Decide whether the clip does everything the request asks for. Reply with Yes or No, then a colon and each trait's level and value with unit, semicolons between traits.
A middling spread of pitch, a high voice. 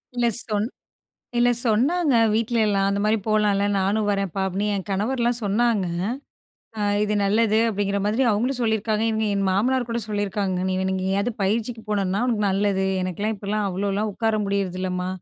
No: narrow, 2.3 semitones; high, 210 Hz